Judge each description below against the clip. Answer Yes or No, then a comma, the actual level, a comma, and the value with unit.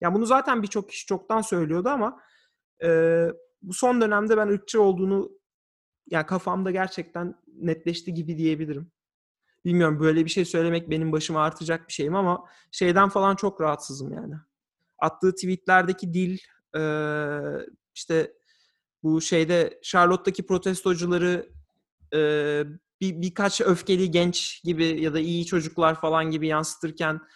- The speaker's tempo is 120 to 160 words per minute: Yes, average, 130 wpm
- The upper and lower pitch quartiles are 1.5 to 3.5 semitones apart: Yes, average, 3.0 semitones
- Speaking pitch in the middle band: Yes, medium, 175 Hz